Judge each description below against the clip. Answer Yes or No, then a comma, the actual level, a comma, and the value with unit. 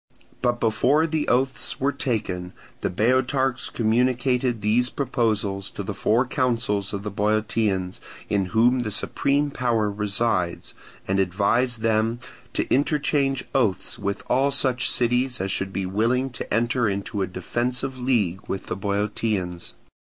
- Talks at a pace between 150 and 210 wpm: No, average, 140 wpm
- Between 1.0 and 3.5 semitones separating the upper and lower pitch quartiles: No, average, 4.1 semitones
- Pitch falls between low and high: No, low, 115 Hz